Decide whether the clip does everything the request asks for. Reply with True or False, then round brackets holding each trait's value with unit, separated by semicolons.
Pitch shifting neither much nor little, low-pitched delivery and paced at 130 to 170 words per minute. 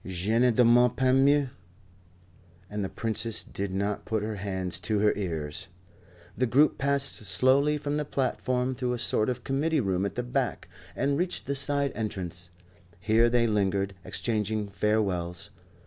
True (4.9 semitones; 115 Hz; 160 wpm)